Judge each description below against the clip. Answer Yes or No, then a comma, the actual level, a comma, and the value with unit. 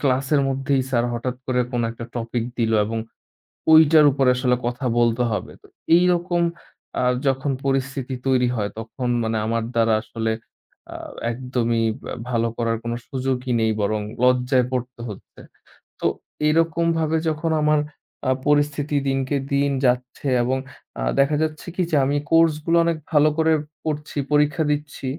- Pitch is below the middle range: Yes, low, 130 Hz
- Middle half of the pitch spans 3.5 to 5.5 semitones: Yes, average, 3.9 semitones